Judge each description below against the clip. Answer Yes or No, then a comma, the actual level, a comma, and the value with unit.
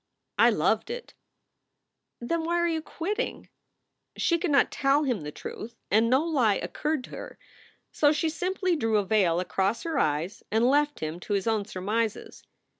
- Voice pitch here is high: Yes, very high, 250 Hz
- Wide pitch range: Yes, wide, 7.6 semitones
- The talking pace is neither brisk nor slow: Yes, average, 175 wpm